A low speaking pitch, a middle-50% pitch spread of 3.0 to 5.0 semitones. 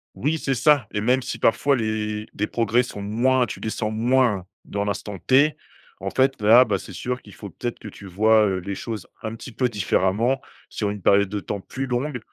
Yes: low, 110 Hz; average, 3.6 semitones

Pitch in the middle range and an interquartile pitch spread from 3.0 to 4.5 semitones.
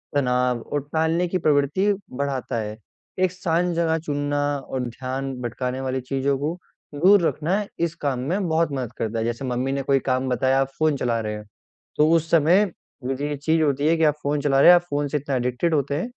Yes: medium, 145 Hz; average, 3.8 semitones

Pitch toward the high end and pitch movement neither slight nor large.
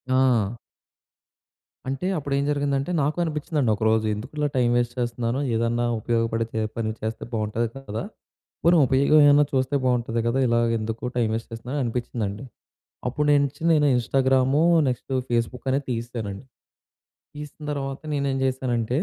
No: low, 125 Hz; average, 3.3 semitones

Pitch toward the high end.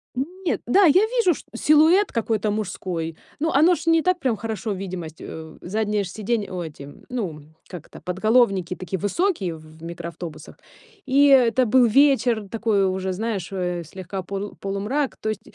Yes: high, 210 Hz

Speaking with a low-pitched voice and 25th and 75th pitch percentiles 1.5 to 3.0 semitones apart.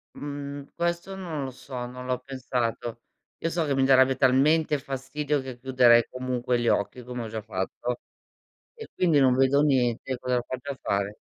Yes: low, 130 Hz; narrow, 2.6 semitones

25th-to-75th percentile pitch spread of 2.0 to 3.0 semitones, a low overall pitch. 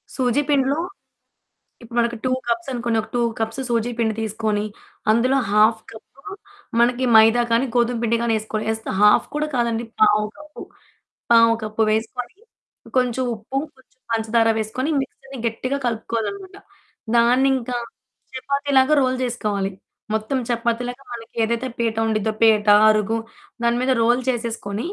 No: narrow, 2.4 semitones; high, 235 Hz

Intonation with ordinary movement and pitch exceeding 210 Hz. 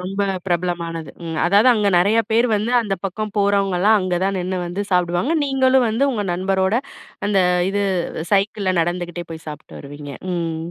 No: average, 3.1 semitones; high, 190 Hz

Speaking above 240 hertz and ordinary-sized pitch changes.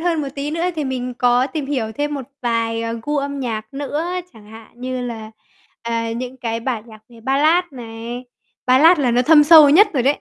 Yes: very high, 255 Hz; average, 4.0 semitones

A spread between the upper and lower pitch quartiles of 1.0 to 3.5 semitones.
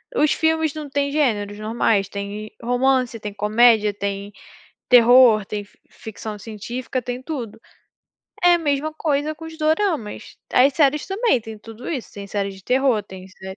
No: wide, 5.6 semitones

